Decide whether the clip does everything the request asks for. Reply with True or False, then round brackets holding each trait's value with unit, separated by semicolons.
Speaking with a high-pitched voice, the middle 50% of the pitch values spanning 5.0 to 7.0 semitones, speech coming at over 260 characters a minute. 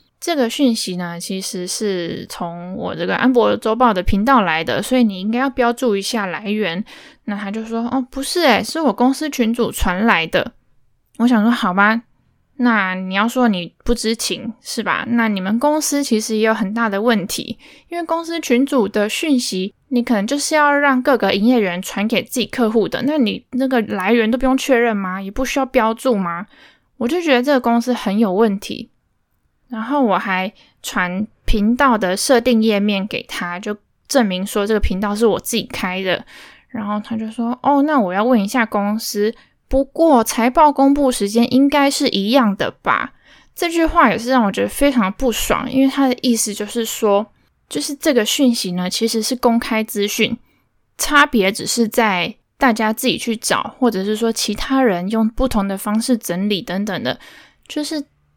False (230 Hz; 4.3 semitones; 270 characters per minute)